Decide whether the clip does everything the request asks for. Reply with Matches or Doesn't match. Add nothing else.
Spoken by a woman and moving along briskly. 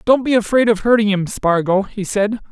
Doesn't match